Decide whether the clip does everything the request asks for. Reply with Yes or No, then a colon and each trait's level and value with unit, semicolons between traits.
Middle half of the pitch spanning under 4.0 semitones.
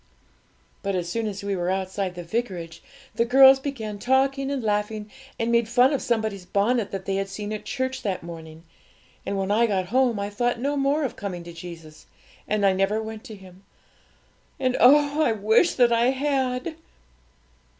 No: average, 4.7 semitones